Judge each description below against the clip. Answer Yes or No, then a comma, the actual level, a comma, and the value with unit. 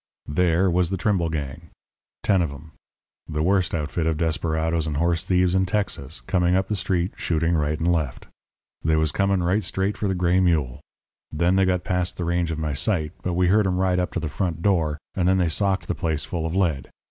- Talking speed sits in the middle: No, fast, 220 wpm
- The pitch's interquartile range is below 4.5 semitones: Yes, average, 2.8 semitones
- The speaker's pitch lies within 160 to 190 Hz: No, very low, 85 Hz